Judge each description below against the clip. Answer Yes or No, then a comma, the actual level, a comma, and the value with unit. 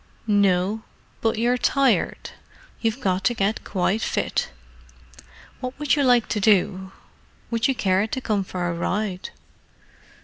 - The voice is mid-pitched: No, high, 215 Hz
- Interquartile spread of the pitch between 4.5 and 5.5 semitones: No, average, 4.0 semitones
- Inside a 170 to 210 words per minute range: No, slow, 135 wpm